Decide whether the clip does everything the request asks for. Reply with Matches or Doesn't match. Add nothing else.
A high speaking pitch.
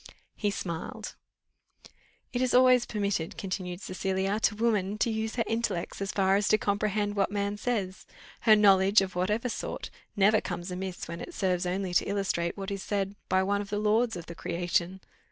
Matches